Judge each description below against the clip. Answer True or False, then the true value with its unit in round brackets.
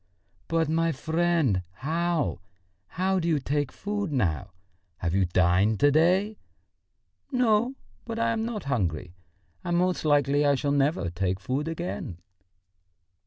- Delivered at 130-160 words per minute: True (135 wpm)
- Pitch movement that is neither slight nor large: False (8.2 semitones)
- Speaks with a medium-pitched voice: True (150 Hz)